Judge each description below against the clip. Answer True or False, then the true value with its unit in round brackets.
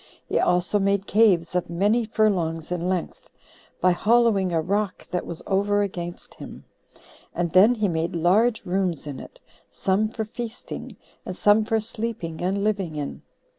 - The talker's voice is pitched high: True (195 Hz)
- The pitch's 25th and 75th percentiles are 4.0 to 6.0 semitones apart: False (3.6 semitones)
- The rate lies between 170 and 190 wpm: False (160 wpm)